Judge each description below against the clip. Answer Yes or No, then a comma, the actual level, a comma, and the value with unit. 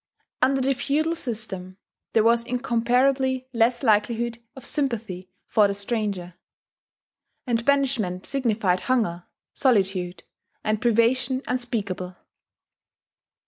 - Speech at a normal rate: No, slow, 100 wpm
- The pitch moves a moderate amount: Yes, average, 4.2 semitones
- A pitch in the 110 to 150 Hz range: No, high, 235 Hz